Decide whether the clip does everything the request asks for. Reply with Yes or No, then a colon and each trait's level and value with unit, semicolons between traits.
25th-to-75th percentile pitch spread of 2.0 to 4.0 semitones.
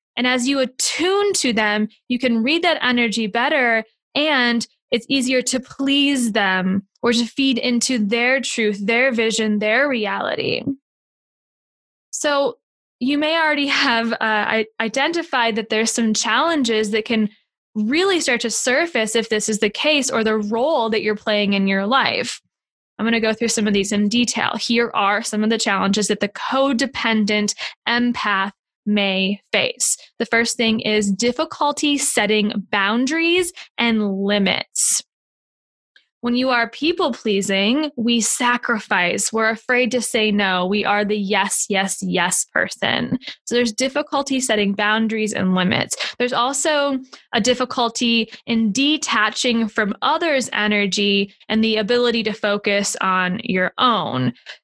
Yes: average, 3.7 semitones